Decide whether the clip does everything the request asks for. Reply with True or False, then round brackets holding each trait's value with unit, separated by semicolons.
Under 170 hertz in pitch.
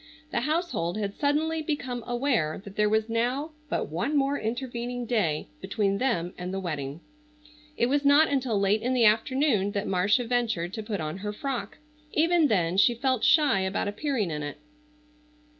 False (230 Hz)